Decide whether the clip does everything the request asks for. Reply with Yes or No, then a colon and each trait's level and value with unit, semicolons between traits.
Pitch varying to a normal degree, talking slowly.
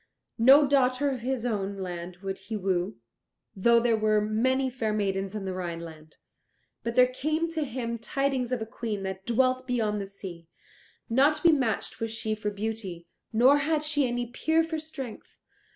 No: average, 4.8 semitones; average, 180 wpm